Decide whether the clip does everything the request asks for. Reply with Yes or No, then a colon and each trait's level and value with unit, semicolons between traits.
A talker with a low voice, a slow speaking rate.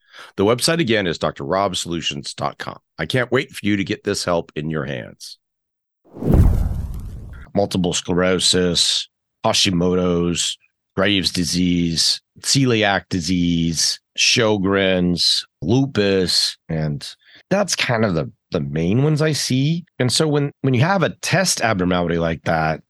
Yes: very low, 95 Hz; slow, 125 wpm